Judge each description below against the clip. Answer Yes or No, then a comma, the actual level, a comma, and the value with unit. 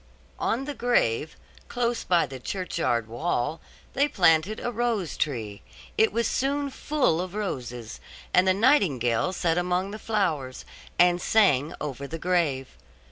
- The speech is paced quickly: No, average, 140 wpm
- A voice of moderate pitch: Yes, medium, 180 Hz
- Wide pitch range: Yes, wide, 8.0 semitones